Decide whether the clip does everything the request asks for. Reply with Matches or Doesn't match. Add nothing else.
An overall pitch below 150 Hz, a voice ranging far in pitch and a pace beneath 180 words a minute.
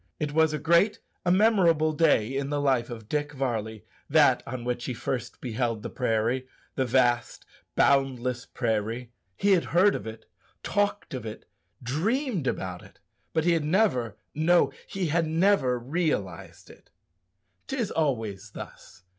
Matches